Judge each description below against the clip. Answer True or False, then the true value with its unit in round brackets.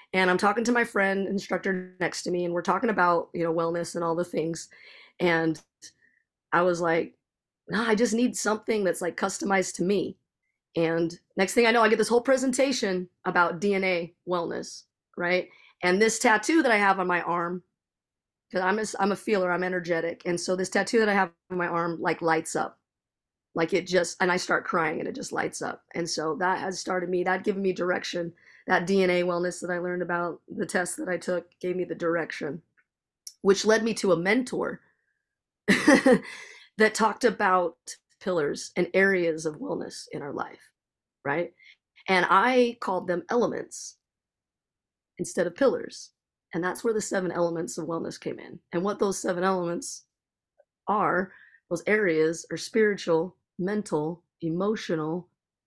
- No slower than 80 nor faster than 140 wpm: False (180 wpm)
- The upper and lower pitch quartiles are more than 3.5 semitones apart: False (2.9 semitones)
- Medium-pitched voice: True (180 Hz)